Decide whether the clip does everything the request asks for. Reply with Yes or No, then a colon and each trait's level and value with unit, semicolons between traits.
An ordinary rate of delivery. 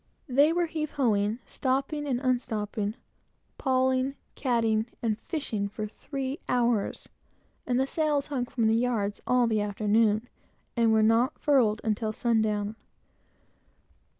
No: slow, 130 wpm